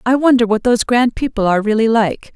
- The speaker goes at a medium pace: No, fast, 230 wpm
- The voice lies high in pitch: Yes, high, 230 Hz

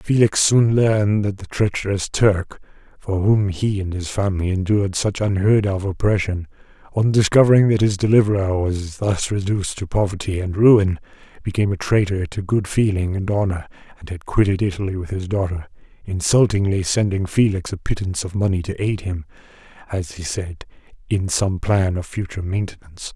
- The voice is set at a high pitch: No, very low, 95 Hz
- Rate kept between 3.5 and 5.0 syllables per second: No, 5.3 syllables/s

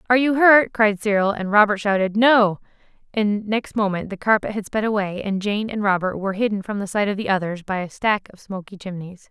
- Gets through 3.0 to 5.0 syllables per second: No, 5.6 syllables/s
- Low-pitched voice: No, high, 205 Hz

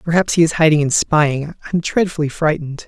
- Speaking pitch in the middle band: Yes, medium, 155 Hz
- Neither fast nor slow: No, fast, 210 wpm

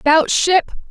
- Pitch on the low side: No, very high, 330 Hz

